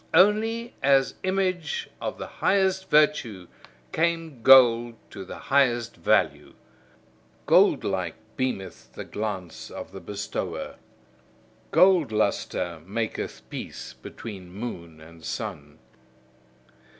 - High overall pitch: No, low, 120 Hz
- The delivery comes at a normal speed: No, slow, 100 wpm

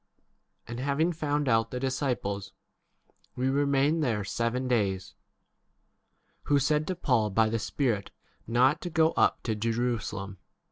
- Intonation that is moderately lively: Yes, average, 4.3 semitones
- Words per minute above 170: No, slow, 135 wpm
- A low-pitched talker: Yes, low, 125 Hz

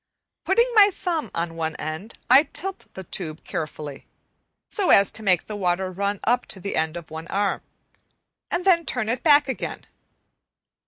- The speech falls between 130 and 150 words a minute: No, average, 170 wpm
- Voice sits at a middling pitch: No, high, 200 Hz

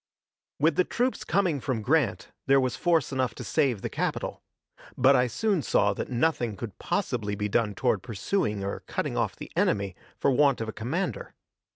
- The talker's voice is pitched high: No, low, 130 Hz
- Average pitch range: No, wide, 6.5 semitones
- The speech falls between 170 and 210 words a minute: Yes, average, 185 wpm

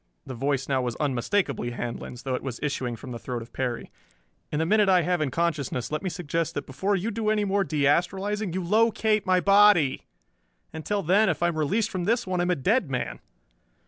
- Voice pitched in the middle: Yes, medium, 170 Hz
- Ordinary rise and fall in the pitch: No, wide, 6.8 semitones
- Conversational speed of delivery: No, fast, 220 wpm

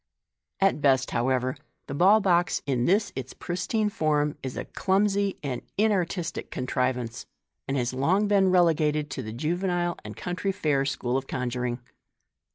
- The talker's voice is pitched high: No, medium, 150 Hz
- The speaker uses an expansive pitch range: Yes, wide, 6.4 semitones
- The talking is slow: No, average, 155 wpm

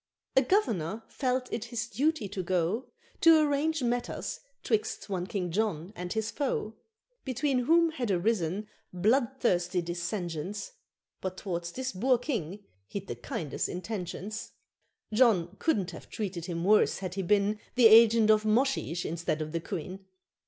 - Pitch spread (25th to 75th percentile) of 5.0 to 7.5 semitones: Yes, wide, 5.6 semitones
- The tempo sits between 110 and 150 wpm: Yes, average, 145 wpm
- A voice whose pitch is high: Yes, high, 210 Hz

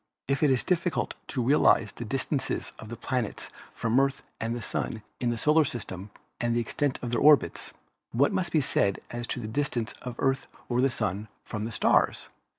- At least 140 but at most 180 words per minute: No, average, 200 wpm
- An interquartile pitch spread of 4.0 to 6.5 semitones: No, average, 3.3 semitones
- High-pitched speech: No, low, 120 Hz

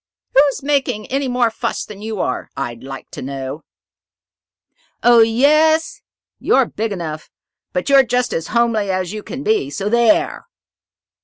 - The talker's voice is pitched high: Yes, high, 225 Hz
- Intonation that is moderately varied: No, wide, 6.3 semitones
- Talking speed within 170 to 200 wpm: No, average, 150 wpm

